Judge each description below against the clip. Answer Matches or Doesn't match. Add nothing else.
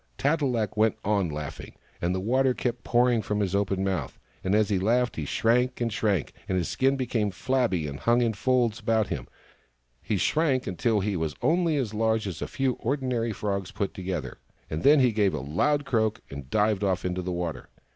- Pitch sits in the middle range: Doesn't match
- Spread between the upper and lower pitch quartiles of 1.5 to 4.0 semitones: Doesn't match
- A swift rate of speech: Matches